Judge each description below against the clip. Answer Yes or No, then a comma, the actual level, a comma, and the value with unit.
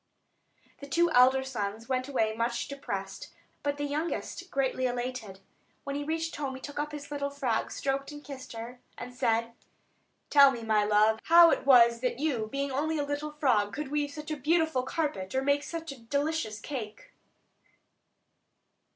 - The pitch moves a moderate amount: Yes, average, 3.9 semitones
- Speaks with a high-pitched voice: Yes, very high, 275 Hz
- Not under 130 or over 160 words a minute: No, average, 175 wpm